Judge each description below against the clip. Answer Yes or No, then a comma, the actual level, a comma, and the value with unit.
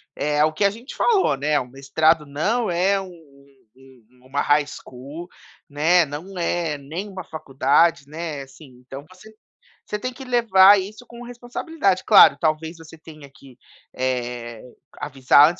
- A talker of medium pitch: Yes, medium, 160 Hz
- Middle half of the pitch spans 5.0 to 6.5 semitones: Yes, wide, 5.6 semitones